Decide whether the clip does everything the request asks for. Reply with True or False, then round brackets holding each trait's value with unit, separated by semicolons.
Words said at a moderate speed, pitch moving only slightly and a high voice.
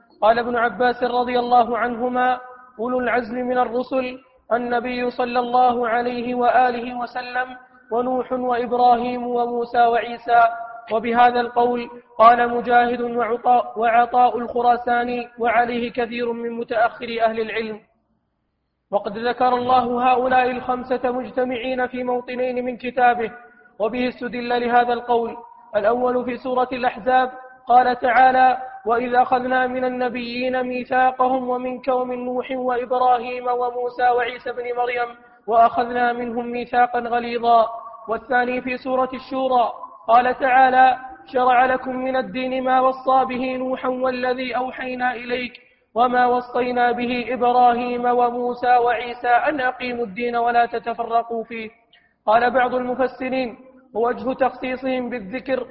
True (110 wpm; 0.9 semitones; 245 Hz)